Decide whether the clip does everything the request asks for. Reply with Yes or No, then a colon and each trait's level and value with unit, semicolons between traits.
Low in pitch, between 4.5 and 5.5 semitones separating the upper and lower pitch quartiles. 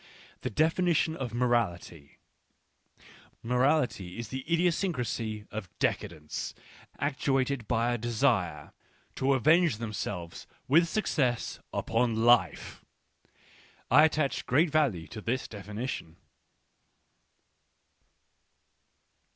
Yes: low, 120 Hz; average, 5.0 semitones